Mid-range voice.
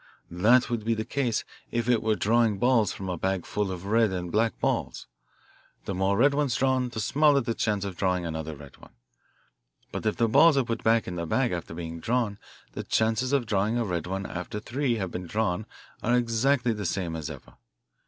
No: low, 110 Hz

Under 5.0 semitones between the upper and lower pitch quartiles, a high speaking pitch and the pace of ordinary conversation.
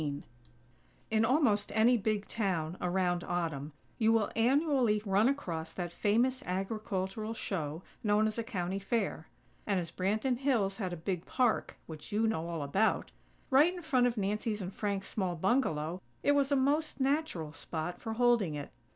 No: average, 5.3 semitones; high, 205 Hz; average, 170 wpm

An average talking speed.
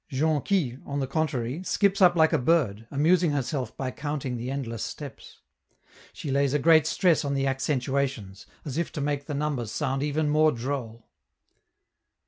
Yes: average, 165 wpm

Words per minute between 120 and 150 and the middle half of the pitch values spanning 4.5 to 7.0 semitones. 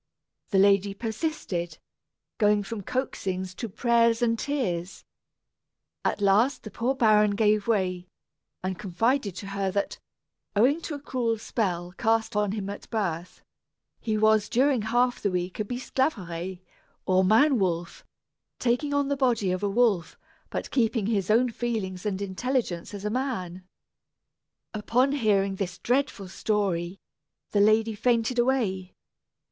No: average, 140 wpm; average, 4.1 semitones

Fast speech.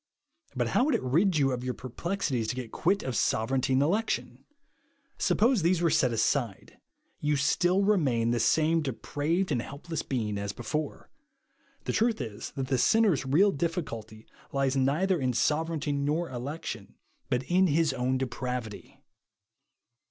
No: average, 155 wpm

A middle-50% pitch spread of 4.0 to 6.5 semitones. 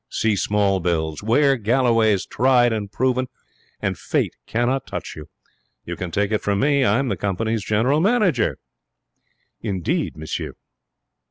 Yes: average, 4.6 semitones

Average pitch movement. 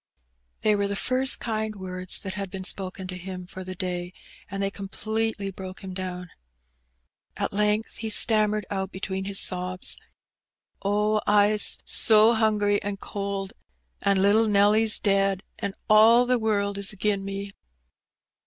No: narrow, 1.9 semitones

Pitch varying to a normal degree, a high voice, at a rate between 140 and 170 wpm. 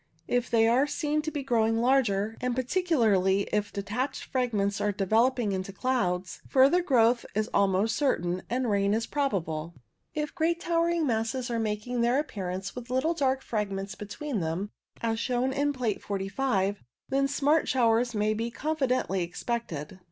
Yes: average, 4.8 semitones; high, 230 Hz; average, 160 wpm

